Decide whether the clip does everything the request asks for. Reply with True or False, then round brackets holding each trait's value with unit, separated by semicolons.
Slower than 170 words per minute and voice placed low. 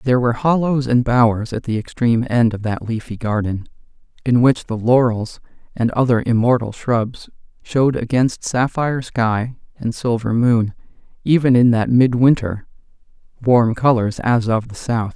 True (150 wpm; 120 Hz)